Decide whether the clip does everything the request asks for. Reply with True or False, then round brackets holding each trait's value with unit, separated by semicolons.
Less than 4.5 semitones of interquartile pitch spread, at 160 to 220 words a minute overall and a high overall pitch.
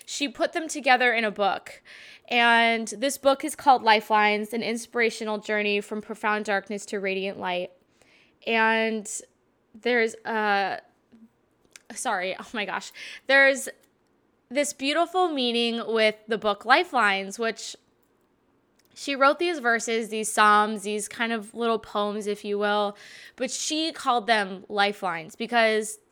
False (2.8 semitones; 135 wpm; 225 Hz)